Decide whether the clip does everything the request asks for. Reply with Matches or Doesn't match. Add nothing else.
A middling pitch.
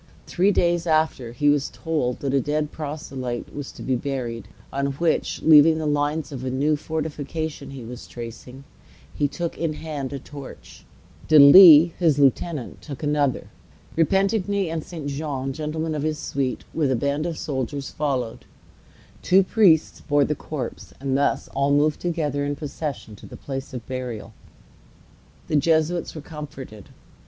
Matches